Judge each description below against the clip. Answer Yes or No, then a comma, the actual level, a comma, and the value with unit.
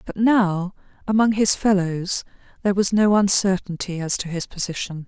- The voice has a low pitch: No, high, 190 Hz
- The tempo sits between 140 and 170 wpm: Yes, average, 155 wpm